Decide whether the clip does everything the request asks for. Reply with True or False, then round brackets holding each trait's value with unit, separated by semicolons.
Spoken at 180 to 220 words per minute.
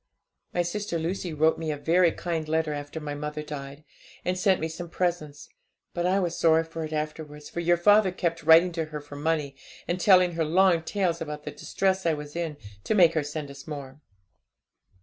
True (205 wpm)